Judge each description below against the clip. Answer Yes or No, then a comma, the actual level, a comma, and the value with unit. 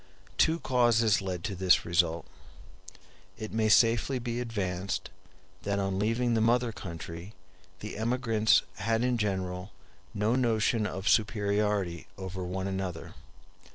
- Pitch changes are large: No, average, 3.5 semitones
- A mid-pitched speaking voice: No, low, 105 Hz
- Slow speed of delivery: Yes, slow, 125 wpm